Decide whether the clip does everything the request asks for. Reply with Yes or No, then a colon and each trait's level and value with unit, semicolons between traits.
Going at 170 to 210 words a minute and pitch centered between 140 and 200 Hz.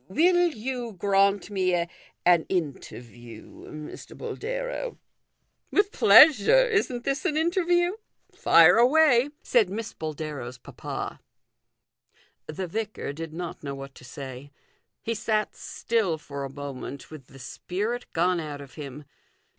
No: slow, 135 wpm; medium, 185 Hz